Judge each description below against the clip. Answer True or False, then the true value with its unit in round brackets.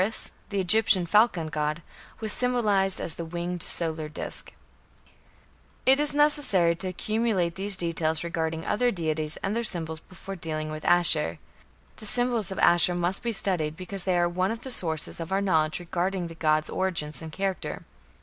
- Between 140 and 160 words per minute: False (170 wpm)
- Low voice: False (175 Hz)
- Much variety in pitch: False (3.7 semitones)